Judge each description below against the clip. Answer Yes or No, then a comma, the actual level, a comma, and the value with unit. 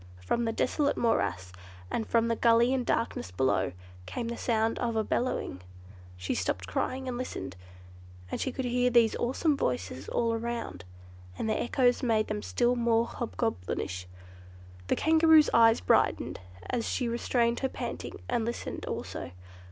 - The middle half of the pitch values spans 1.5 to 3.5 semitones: Yes, narrow, 2.5 semitones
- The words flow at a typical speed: Yes, average, 150 wpm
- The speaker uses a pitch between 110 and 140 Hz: No, high, 235 Hz